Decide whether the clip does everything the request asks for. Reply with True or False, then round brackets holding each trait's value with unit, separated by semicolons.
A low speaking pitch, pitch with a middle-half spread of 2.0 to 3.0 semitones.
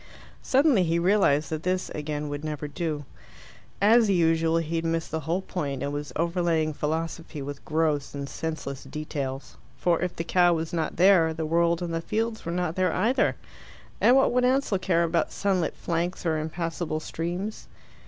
False (165 Hz; 2.7 semitones)